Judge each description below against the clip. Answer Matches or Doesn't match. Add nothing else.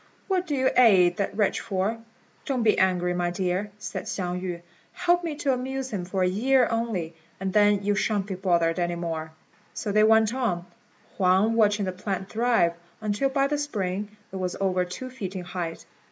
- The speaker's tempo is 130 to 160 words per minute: Doesn't match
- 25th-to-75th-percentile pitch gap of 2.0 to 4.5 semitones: Matches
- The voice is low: Doesn't match